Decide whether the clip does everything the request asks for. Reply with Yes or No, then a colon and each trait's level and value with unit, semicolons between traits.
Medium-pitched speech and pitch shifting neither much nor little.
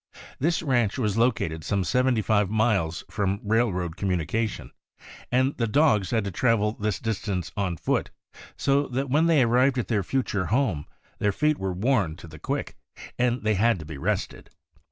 No: low, 110 Hz; average, 4.9 semitones